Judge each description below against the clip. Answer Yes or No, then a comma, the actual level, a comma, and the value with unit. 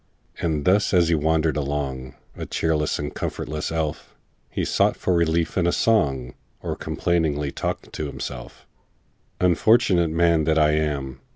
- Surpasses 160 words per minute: No, average, 150 wpm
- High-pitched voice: No, very low, 80 Hz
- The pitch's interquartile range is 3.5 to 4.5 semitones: No, narrow, 2.6 semitones